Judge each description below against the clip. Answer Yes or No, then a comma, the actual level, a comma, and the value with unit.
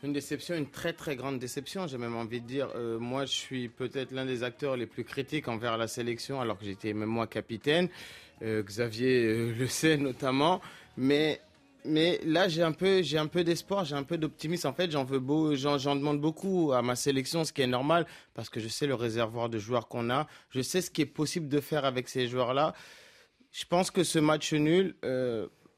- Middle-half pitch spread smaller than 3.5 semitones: No, average, 4.3 semitones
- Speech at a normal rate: No, fast, 225 wpm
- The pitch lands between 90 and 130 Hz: No, medium, 140 Hz